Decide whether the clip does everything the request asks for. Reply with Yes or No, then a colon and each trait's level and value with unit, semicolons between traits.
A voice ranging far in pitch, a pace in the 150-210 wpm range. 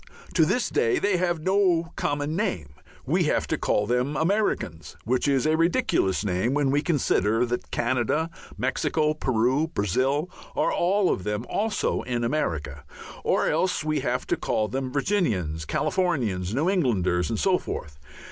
Yes: wide, 8.0 semitones; average, 155 wpm